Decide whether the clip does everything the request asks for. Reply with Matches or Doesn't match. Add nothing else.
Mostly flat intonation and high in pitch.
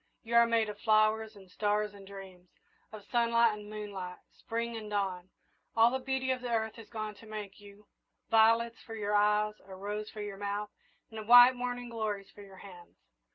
Matches